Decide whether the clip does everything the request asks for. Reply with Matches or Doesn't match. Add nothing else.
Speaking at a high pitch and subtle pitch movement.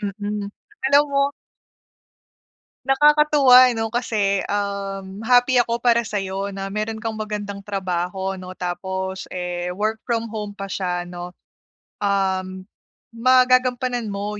Doesn't match